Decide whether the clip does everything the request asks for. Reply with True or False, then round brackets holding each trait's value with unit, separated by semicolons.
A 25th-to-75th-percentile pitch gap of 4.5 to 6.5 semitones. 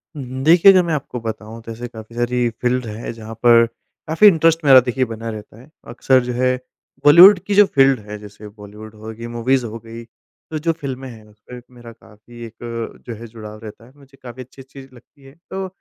False (3.2 semitones)